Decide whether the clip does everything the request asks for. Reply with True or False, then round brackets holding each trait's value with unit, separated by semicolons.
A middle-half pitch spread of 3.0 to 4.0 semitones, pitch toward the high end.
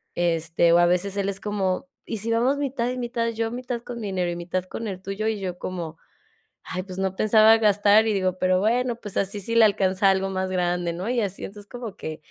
True (3.5 semitones; 200 Hz)